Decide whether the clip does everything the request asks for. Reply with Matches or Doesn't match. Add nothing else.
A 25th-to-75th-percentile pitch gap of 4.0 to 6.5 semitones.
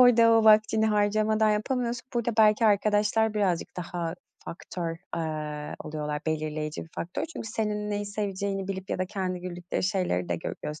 Matches